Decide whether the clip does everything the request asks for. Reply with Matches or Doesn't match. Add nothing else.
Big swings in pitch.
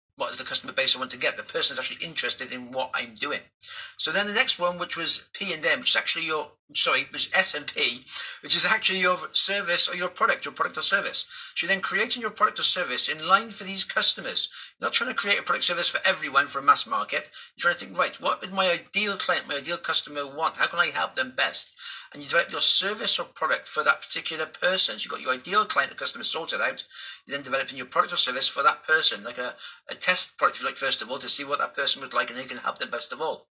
Matches